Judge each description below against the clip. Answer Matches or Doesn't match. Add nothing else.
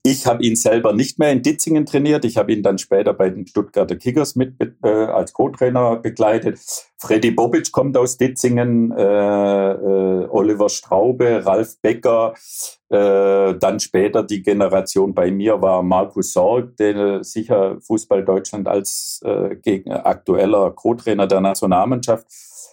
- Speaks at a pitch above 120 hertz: Doesn't match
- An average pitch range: Matches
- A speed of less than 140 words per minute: Doesn't match